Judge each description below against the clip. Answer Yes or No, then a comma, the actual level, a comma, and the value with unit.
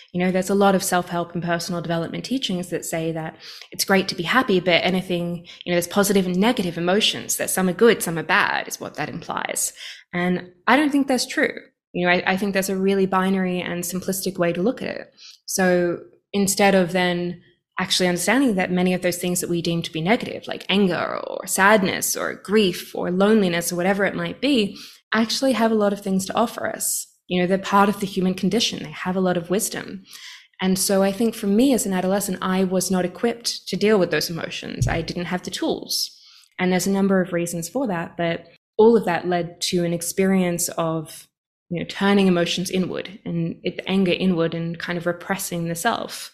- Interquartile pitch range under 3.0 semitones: Yes, narrow, 2.5 semitones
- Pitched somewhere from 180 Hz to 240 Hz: Yes, medium, 185 Hz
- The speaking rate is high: Yes, fast, 220 wpm